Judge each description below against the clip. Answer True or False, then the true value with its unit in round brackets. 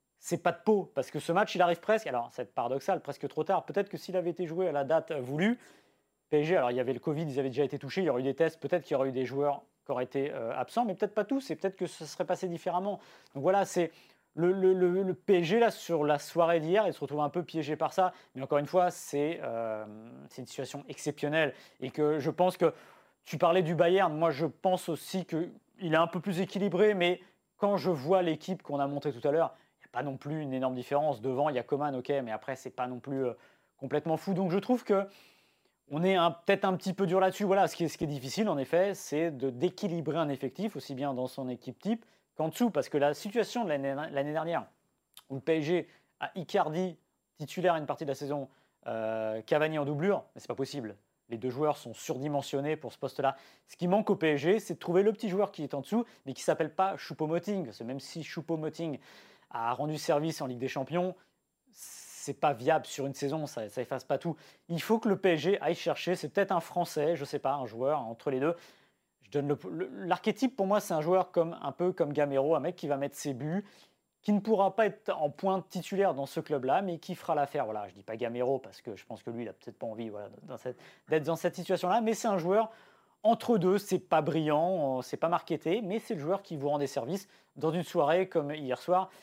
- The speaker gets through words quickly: True (245 wpm)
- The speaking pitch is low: False (160 Hz)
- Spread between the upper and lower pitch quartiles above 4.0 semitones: True (4.8 semitones)